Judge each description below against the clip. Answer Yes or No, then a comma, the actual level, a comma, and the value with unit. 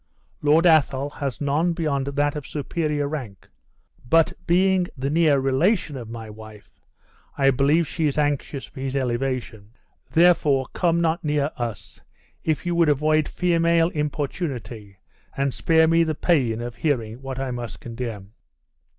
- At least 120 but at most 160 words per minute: Yes, average, 150 wpm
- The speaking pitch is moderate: Yes, medium, 145 Hz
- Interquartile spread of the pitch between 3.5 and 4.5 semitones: Yes, average, 4.2 semitones